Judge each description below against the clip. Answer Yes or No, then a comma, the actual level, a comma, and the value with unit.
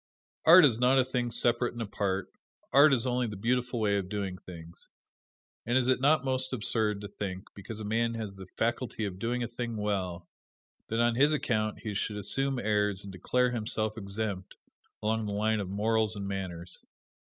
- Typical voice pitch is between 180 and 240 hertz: No, low, 110 Hz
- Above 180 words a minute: Yes, average, 190 wpm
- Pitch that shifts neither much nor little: Yes, average, 3.4 semitones